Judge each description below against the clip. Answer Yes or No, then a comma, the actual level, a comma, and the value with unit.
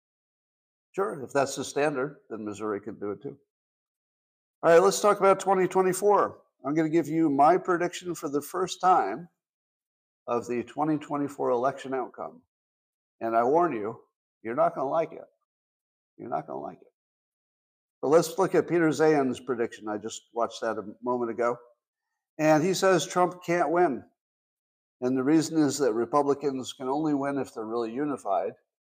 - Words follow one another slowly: No, average, 170 wpm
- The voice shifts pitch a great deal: Yes, wide, 6.3 semitones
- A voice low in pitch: No, medium, 145 Hz